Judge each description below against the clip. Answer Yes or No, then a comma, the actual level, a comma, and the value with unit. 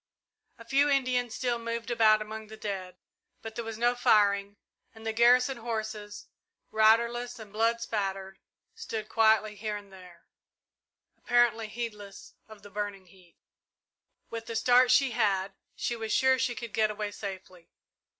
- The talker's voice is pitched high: Yes, high, 220 Hz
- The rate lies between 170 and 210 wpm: No, average, 150 wpm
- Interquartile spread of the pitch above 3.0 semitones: No, narrow, 2.5 semitones